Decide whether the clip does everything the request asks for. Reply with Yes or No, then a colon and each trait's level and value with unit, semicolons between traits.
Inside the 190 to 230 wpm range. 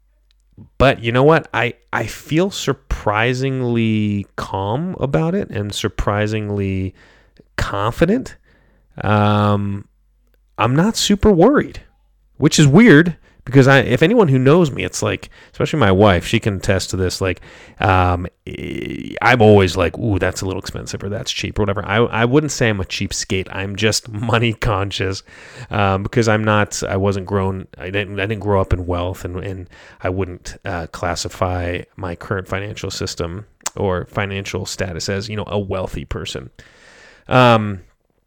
No: average, 155 wpm